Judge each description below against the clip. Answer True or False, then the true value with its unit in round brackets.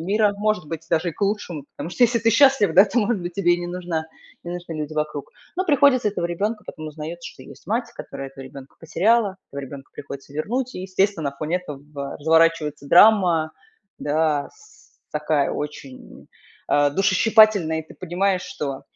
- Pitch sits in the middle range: True (175 Hz)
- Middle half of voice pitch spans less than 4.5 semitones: False (5.5 semitones)